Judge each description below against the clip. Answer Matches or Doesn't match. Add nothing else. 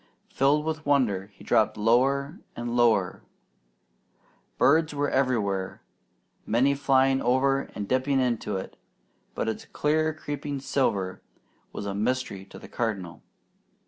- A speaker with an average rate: Doesn't match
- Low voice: Matches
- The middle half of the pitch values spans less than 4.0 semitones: Doesn't match